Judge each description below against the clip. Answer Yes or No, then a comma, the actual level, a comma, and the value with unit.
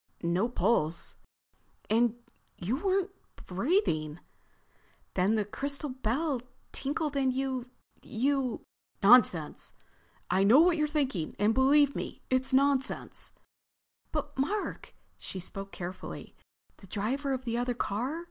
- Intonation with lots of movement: Yes, wide, 5.8 semitones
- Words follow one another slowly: Yes, slow, 110 wpm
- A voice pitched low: No, very high, 255 Hz